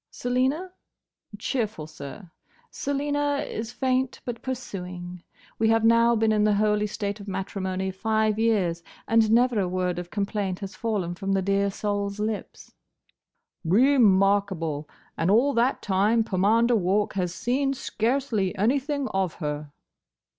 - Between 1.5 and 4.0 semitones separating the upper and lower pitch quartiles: Yes, average, 3.7 semitones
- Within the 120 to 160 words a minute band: Yes, average, 140 wpm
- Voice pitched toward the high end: Yes, high, 210 Hz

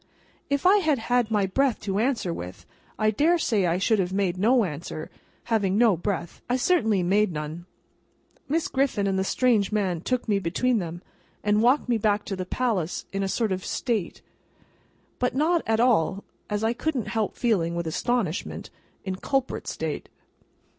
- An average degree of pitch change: Yes, average, 4.9 semitones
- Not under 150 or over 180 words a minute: Yes, average, 175 wpm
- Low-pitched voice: No, high, 210 Hz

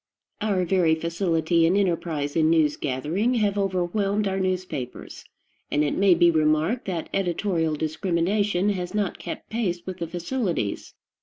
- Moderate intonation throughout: Yes, average, 3.5 semitones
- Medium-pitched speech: Yes, medium, 175 Hz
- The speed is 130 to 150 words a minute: Yes, average, 145 wpm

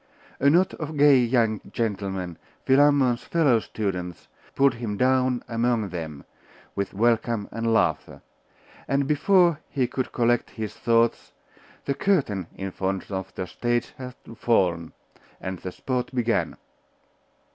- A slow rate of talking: Yes, slow, 130 wpm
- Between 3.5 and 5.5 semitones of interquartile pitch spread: Yes, average, 5.0 semitones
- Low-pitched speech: Yes, low, 120 Hz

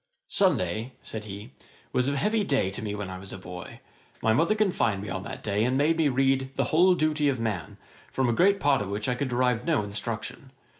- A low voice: Yes, low, 125 Hz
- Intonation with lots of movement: Yes, wide, 5.7 semitones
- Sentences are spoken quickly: Yes, fast, 230 wpm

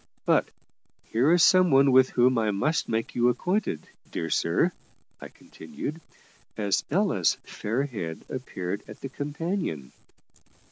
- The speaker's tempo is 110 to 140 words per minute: Yes, slow, 135 wpm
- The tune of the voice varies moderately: No, wide, 6.9 semitones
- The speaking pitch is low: Yes, low, 130 Hz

